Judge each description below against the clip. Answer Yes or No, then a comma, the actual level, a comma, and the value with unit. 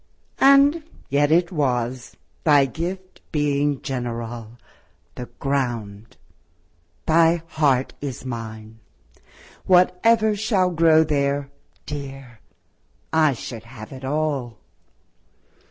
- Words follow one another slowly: Yes, slow, 95 wpm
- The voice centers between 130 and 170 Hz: Yes, medium, 140 Hz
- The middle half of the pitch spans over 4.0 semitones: Yes, average, 5.1 semitones